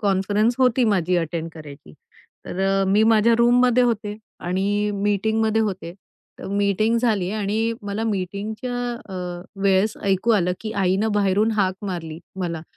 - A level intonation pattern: No, average, 3.0 semitones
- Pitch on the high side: Yes, high, 200 Hz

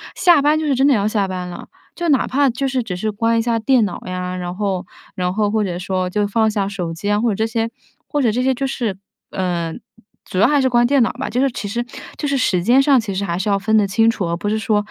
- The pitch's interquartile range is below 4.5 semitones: No, average, 4.8 semitones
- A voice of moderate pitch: No, high, 215 Hz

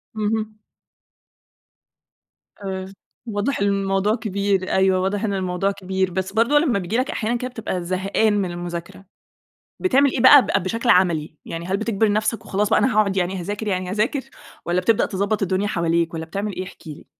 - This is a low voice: No, high, 195 Hz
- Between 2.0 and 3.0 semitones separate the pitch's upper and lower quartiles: Yes, average, 2.7 semitones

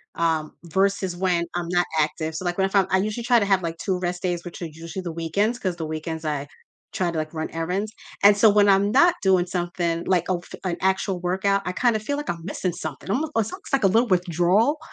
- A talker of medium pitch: Yes, medium, 180 Hz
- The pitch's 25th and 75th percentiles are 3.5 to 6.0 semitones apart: No, average, 3.1 semitones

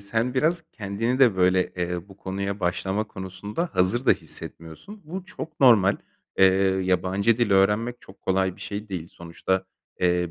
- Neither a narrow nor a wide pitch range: Yes, average, 4.0 semitones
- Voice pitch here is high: No, low, 100 Hz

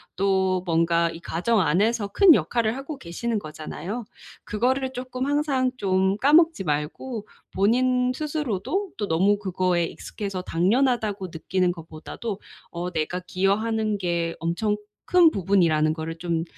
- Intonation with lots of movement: Yes, wide, 6.4 semitones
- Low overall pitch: No, high, 200 Hz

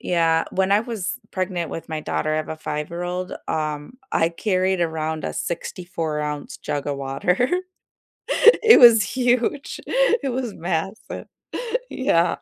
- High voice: No, medium, 175 Hz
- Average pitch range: No, wide, 5.7 semitones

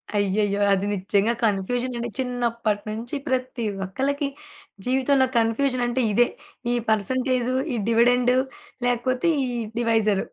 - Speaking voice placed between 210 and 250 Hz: Yes, high, 240 Hz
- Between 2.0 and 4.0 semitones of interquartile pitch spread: Yes, average, 3.1 semitones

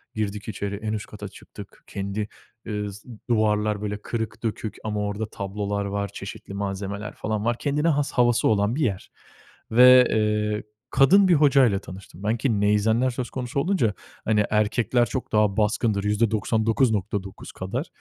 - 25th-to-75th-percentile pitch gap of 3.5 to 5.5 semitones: No, average, 2.7 semitones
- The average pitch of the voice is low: Yes, low, 105 Hz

